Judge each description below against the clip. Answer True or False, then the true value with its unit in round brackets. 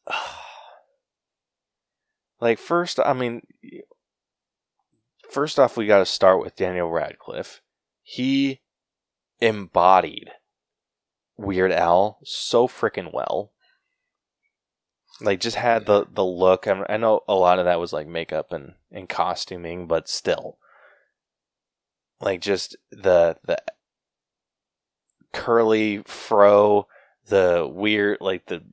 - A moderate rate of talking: False (110 wpm)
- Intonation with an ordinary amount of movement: False (6.6 semitones)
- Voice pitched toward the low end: True (105 Hz)